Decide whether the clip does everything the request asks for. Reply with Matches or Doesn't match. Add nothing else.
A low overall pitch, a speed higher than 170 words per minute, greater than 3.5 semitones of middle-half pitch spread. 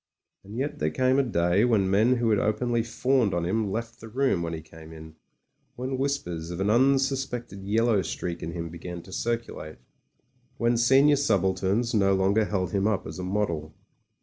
Matches